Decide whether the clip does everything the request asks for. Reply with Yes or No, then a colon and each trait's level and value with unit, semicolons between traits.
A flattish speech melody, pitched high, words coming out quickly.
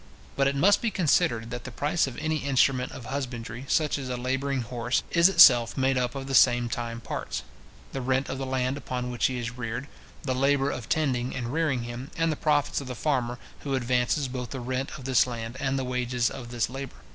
No: narrow, 2.1 semitones; low, 130 Hz; fast, 225 wpm